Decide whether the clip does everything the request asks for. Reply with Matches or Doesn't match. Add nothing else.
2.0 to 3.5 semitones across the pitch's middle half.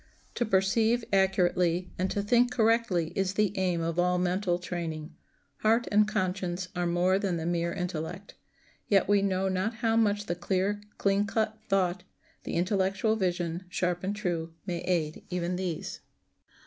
Matches